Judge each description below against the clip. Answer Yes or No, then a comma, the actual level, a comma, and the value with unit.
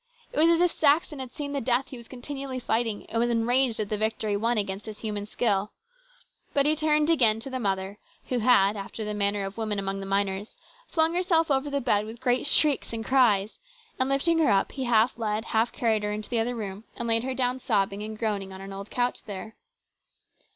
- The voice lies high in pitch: Yes, high, 230 Hz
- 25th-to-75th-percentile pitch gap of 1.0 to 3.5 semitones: No, average, 4.1 semitones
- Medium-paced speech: No, fast, 225 wpm